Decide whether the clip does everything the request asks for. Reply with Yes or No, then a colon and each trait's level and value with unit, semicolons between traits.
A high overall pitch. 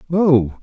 No: medium, 140 Hz